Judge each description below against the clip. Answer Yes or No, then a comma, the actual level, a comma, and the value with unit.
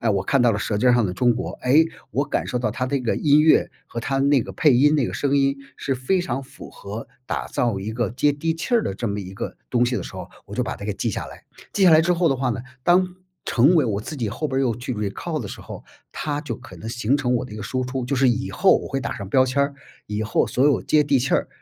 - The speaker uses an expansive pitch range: No, average, 3.7 semitones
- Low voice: Yes, low, 130 Hz